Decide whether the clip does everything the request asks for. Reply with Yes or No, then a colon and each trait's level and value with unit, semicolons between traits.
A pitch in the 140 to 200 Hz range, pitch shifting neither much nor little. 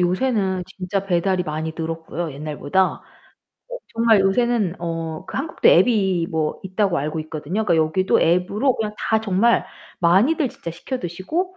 Yes: medium, 185 Hz; average, 4.7 semitones